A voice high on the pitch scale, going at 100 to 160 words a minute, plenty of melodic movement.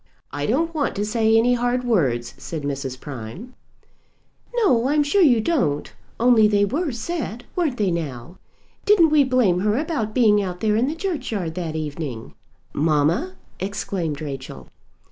Yes: high, 215 Hz; average, 155 wpm; wide, 8.6 semitones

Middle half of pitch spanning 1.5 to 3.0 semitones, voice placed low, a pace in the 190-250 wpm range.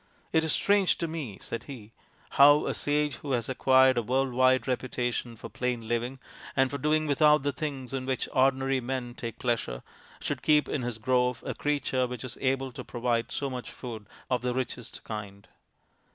Yes: narrow, 2.4 semitones; low, 130 Hz; average, 195 wpm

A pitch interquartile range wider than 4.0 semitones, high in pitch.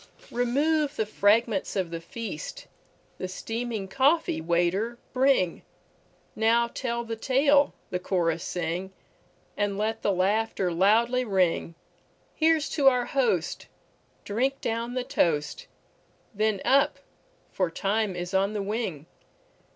Yes: average, 5.1 semitones; high, 220 Hz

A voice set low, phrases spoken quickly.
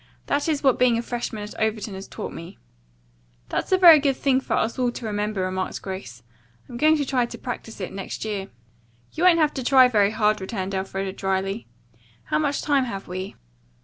No: high, 220 Hz; fast, 210 wpm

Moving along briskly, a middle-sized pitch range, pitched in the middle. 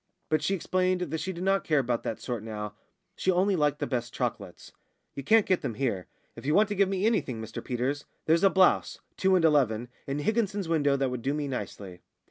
No: fast, 225 wpm; wide, 7.1 semitones; medium, 150 Hz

